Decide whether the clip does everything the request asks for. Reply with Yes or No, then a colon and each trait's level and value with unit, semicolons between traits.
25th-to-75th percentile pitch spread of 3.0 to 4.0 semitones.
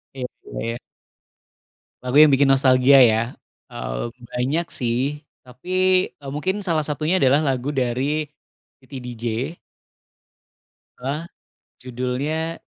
Yes: average, 3.3 semitones